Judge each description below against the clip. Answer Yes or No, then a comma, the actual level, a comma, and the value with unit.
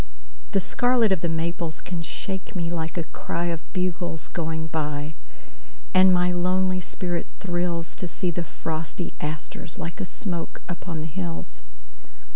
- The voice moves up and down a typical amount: No, narrow, 2.2 semitones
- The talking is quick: No, slow, 135 wpm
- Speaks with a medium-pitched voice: Yes, medium, 170 Hz